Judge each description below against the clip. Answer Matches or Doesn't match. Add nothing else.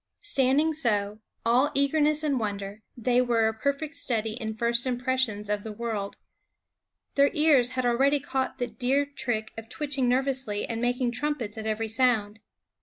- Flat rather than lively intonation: Doesn't match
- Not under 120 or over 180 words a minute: Matches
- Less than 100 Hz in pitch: Doesn't match